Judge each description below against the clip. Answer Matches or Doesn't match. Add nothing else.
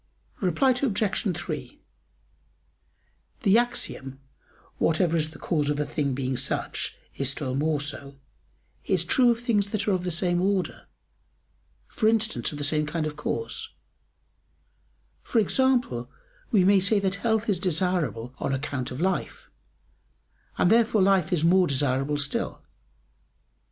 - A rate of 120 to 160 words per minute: Matches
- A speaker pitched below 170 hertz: Doesn't match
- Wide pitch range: Matches